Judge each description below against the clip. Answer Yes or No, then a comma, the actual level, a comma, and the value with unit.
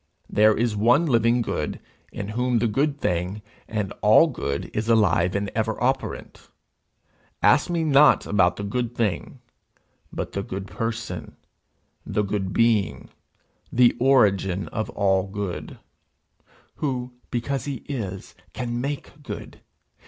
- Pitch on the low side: Yes, low, 110 Hz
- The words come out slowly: Yes, slow, 130 wpm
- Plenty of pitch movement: No, average, 3.9 semitones